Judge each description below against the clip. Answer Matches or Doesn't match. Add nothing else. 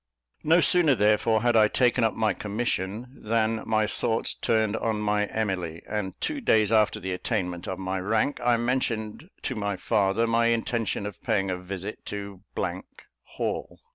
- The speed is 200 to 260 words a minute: Doesn't match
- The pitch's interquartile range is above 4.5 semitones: Doesn't match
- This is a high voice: Doesn't match